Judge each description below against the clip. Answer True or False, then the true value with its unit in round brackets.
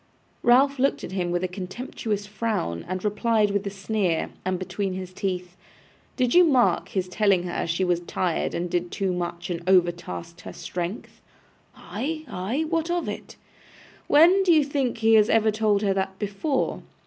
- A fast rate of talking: False (170 wpm)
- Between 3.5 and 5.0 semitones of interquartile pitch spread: True (4.7 semitones)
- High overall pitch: True (200 Hz)